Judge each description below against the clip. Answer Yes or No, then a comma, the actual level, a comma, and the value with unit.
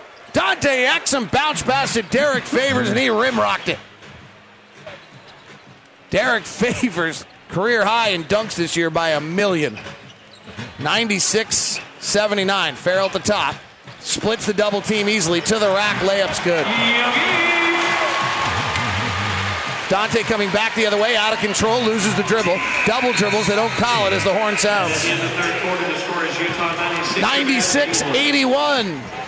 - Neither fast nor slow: No, slow, 125 wpm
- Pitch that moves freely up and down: No, average, 4.1 semitones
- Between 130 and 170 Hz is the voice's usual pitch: No, high, 210 Hz